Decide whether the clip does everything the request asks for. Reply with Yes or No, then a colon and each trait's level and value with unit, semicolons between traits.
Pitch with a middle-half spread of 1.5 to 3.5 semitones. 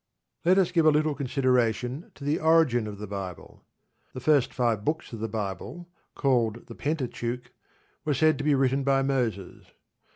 No: average, 4.8 semitones